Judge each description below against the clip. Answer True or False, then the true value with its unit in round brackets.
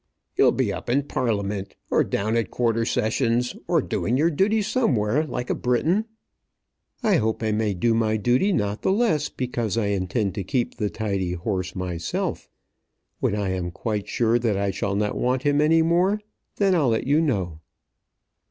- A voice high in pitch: False (115 Hz)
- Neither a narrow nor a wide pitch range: False (6.1 semitones)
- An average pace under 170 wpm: False (180 wpm)